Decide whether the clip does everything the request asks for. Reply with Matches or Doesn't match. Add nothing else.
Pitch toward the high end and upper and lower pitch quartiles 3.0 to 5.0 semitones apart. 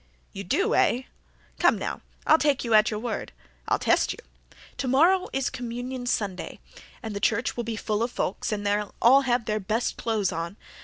Matches